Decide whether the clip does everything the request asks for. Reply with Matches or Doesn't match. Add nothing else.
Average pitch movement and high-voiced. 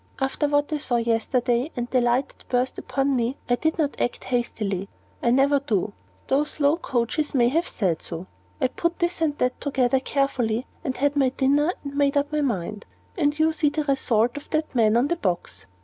Matches